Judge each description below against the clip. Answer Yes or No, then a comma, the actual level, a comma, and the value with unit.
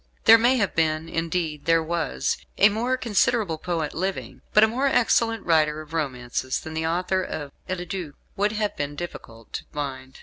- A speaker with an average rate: Yes, average, 180 wpm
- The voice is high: No, medium, 165 Hz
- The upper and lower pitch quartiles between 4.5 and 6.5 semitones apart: Yes, average, 5.2 semitones